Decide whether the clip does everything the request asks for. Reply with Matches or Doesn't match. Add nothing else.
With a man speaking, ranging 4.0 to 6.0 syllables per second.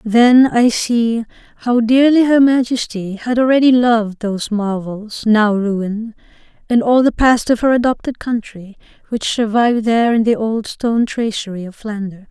Doesn't match